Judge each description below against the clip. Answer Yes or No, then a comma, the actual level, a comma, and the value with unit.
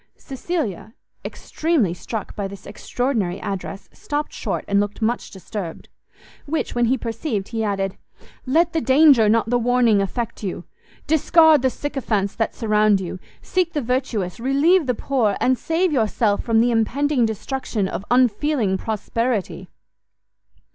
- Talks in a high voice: Yes, high, 230 Hz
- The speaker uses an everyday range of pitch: Yes, average, 4.9 semitones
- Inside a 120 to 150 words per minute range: Yes, average, 140 wpm